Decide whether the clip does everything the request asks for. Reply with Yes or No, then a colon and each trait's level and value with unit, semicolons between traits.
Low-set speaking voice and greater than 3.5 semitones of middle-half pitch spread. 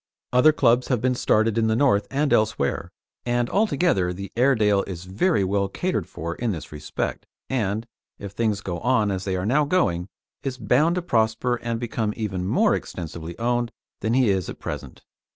Yes: low, 110 Hz; average, 4.4 semitones